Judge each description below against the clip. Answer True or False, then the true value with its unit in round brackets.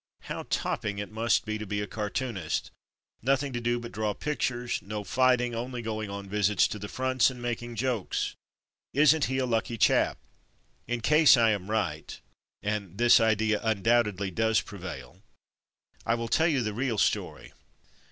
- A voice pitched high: False (115 Hz)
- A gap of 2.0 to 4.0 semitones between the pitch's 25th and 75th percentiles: True (2.9 semitones)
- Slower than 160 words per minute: False (170 wpm)